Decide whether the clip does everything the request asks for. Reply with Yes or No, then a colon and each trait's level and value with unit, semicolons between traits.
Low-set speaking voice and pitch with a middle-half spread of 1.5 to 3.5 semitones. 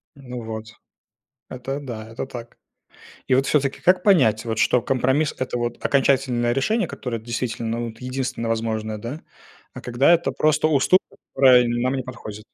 Yes: low, 125 Hz; average, 2.9 semitones